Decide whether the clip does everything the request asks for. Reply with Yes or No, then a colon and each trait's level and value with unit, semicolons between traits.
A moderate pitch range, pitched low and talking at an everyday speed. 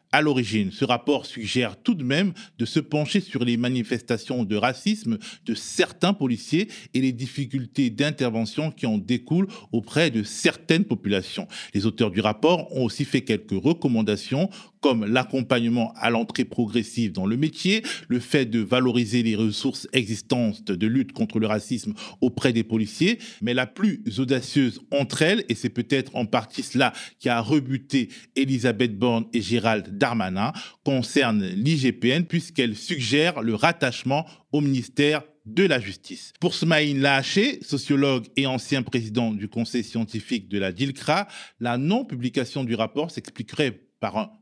Yes: average, 4.5 semitones; low, 130 Hz; average, 155 wpm